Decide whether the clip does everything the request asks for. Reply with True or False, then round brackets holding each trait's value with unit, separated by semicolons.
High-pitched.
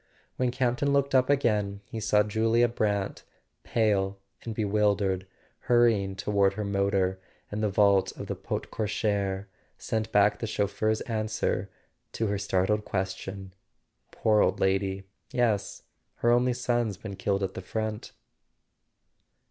False (105 Hz)